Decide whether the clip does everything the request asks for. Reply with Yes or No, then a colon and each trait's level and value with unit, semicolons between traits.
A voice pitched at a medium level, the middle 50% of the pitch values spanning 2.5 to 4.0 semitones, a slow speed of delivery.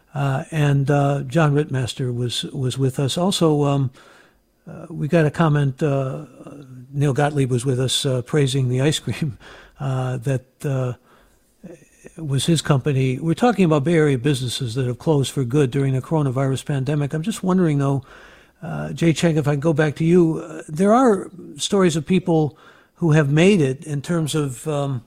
No: medium, 145 Hz; average, 3.4 semitones; average, 180 wpm